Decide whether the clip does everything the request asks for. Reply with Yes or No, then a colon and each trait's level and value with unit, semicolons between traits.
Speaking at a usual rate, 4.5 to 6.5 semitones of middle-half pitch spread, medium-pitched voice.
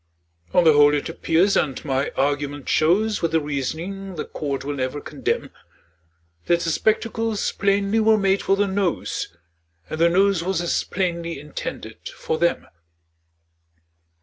Yes: average, 150 wpm; average, 5.0 semitones; medium, 170 Hz